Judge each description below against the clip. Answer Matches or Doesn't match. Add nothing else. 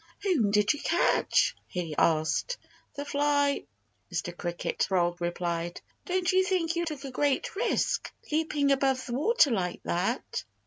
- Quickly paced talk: Doesn't match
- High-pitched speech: Matches